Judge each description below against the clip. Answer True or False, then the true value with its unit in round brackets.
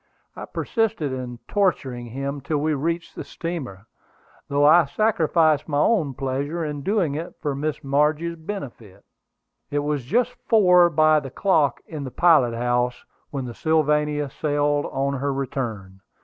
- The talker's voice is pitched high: False (145 Hz)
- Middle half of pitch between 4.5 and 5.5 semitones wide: False (3.4 semitones)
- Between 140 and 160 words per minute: True (150 wpm)